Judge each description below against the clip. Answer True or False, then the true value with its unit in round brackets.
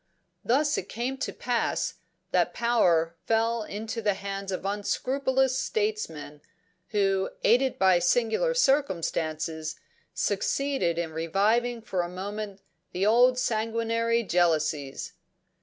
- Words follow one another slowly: True (110 wpm)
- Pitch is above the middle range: True (215 Hz)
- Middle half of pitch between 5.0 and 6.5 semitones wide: True (5.5 semitones)